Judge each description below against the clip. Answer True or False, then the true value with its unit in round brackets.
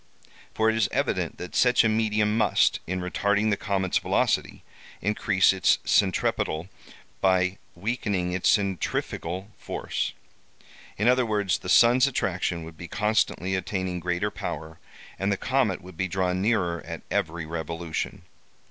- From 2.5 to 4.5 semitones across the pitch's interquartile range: True (3.1 semitones)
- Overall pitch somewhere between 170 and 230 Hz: False (95 Hz)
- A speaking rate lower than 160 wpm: True (140 wpm)